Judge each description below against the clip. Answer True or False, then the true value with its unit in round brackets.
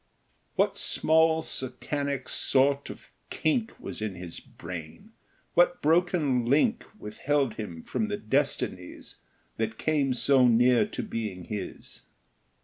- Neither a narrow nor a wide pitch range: False (6.4 semitones)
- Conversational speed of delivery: False (120 wpm)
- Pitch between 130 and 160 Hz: True (135 Hz)